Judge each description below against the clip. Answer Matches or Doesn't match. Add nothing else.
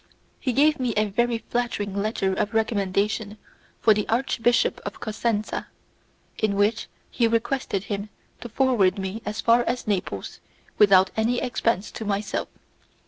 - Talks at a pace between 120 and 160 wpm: Matches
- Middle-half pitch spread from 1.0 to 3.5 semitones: Matches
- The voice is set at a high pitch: Matches